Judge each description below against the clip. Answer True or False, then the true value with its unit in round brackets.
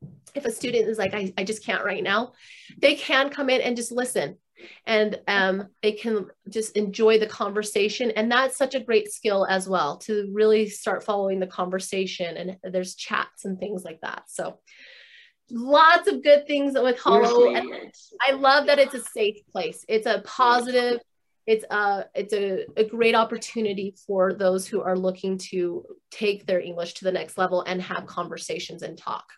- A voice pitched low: False (215 Hz)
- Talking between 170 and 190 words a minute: True (180 wpm)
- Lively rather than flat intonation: False (4.7 semitones)